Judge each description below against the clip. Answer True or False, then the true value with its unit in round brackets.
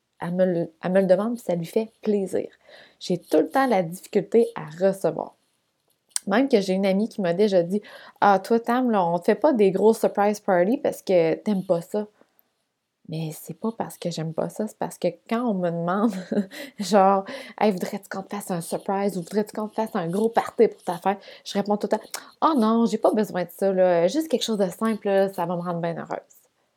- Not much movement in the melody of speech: False (3.7 semitones)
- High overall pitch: True (200 Hz)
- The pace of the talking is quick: True (230 wpm)